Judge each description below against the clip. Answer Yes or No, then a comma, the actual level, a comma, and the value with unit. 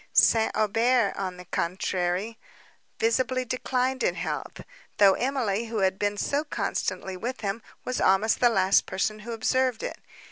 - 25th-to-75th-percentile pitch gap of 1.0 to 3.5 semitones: No, average, 4.4 semitones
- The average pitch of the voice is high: Yes, high, 220 Hz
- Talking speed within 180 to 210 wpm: No, average, 150 wpm